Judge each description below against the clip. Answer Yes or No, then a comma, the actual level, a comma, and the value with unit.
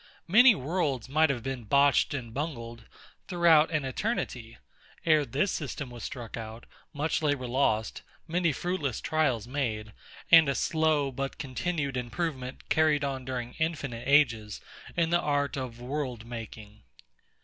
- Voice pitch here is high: No, medium, 140 Hz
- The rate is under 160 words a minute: Yes, average, 140 wpm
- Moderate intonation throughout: Yes, average, 4.5 semitones